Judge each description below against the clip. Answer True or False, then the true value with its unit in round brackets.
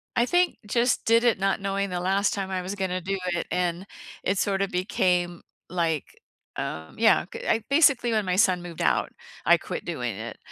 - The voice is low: False (195 Hz)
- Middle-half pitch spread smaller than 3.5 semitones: True (2.9 semitones)